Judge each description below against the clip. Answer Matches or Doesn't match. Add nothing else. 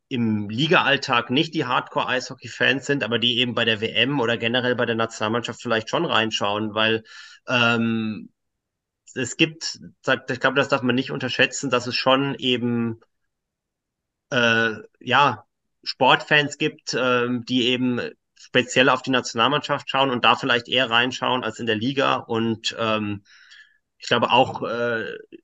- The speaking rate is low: Doesn't match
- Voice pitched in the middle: Doesn't match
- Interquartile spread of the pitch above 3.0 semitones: Doesn't match